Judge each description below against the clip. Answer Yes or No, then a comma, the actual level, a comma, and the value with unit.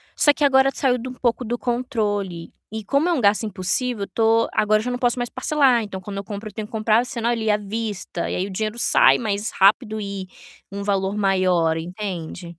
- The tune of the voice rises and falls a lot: No, average, 3.4 semitones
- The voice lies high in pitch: Yes, high, 215 Hz